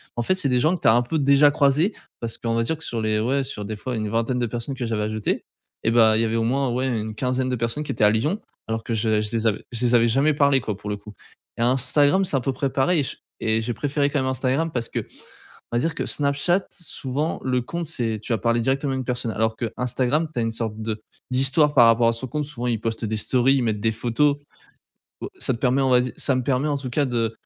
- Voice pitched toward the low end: Yes, low, 125 Hz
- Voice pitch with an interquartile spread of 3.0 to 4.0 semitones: Yes, average, 3.6 semitones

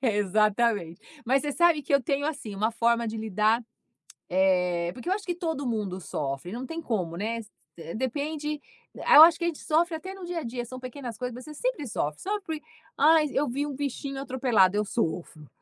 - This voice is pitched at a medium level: No, very high, 250 Hz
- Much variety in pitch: Yes, wide, 6.1 semitones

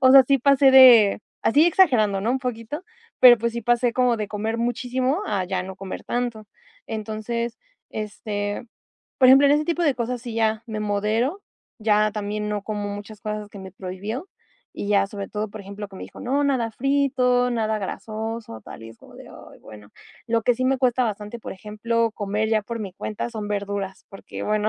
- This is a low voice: No, high, 220 Hz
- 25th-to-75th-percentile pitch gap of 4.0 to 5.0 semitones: No, average, 3.2 semitones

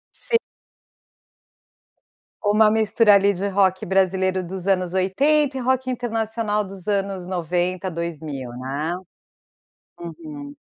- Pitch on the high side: Yes, high, 195 Hz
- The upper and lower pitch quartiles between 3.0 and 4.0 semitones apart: Yes, average, 3.7 semitones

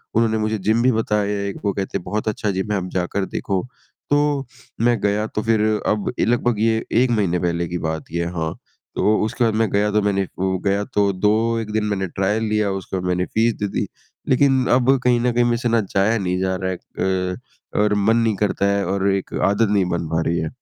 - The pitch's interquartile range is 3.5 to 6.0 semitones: No, average, 3.0 semitones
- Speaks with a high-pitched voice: No, low, 105 Hz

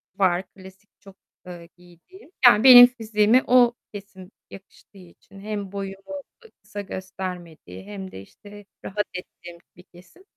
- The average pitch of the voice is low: No, high, 195 Hz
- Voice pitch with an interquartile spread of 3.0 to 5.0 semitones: No, narrow, 2.5 semitones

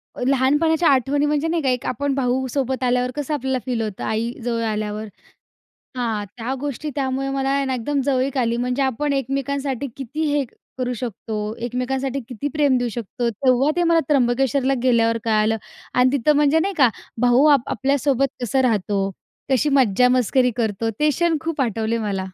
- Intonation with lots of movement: No, average, 3.1 semitones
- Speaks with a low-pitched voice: No, very high, 260 Hz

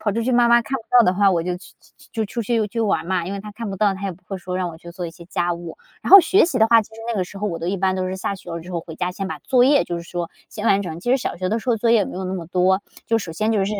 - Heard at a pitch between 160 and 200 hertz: Yes, high, 195 Hz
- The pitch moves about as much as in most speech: Yes, average, 4.1 semitones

